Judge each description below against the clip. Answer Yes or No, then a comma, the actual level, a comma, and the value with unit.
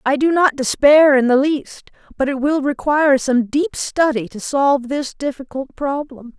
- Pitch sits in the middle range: No, very high, 275 Hz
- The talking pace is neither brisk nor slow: Yes, average, 180 wpm